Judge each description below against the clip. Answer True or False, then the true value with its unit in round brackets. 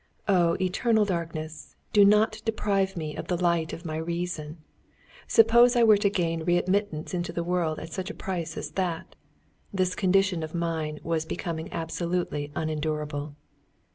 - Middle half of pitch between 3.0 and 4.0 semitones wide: True (3.4 semitones)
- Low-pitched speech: False (175 Hz)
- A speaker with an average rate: True (155 wpm)